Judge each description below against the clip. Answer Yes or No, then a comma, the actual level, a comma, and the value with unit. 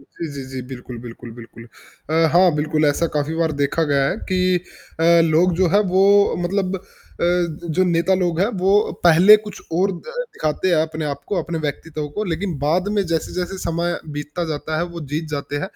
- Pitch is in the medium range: Yes, medium, 165 Hz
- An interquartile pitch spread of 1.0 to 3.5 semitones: Yes, average, 3.2 semitones